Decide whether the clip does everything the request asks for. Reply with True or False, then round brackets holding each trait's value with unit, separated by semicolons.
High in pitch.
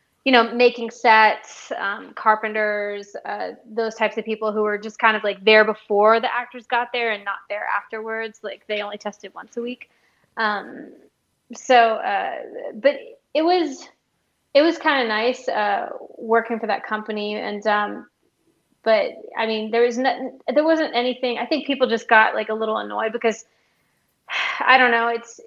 True (230 Hz)